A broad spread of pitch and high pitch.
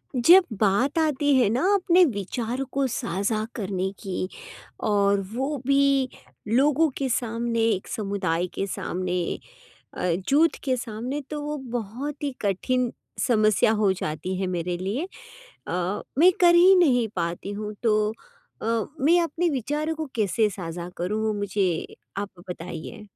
Yes: wide, 6.3 semitones; high, 225 Hz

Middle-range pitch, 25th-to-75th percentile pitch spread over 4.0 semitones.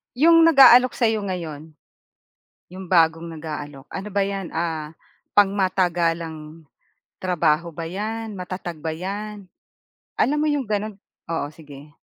Yes: medium, 180 Hz; average, 4.4 semitones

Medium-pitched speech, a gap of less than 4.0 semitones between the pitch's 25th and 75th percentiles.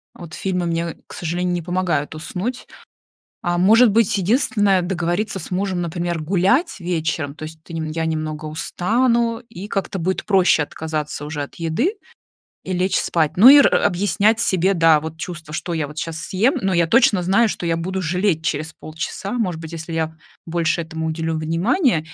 Yes: medium, 175 Hz; average, 3.4 semitones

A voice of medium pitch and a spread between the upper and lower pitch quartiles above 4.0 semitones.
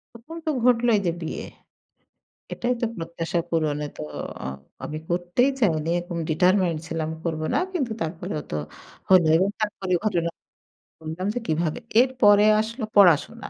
Yes: medium, 180 Hz; average, 5.1 semitones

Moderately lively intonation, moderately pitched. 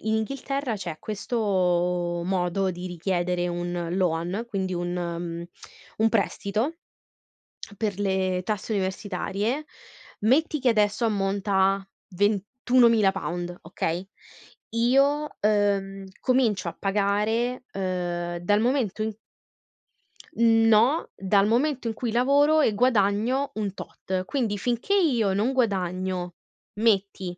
No: average, 4.2 semitones; high, 200 Hz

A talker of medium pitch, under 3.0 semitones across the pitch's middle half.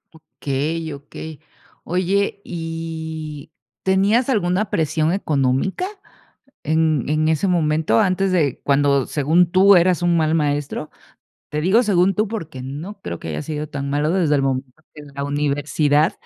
No: medium, 160 Hz; average, 3.8 semitones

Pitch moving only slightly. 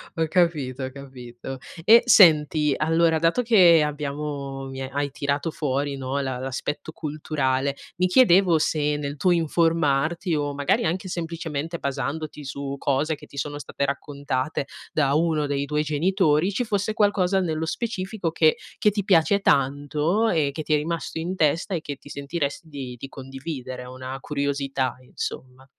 No: average, 3.3 semitones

